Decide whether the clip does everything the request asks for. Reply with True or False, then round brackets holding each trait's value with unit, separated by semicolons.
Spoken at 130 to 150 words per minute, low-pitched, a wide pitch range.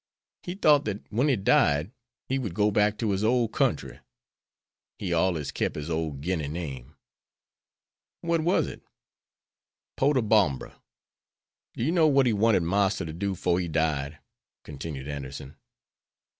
True (145 wpm; 95 Hz; 6.9 semitones)